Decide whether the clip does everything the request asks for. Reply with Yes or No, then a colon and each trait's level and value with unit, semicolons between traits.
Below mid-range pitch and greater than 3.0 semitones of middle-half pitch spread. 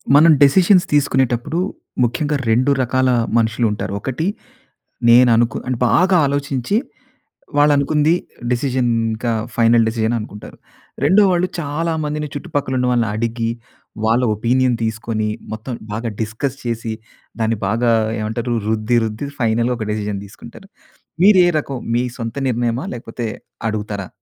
Yes: low, 120 Hz; average, 4.1 semitones